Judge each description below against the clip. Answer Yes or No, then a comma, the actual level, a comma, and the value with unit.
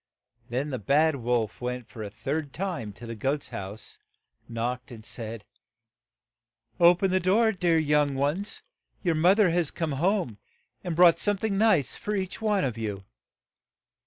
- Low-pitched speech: No, medium, 150 Hz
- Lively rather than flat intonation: Yes, wide, 7.3 semitones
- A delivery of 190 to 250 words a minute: No, average, 165 wpm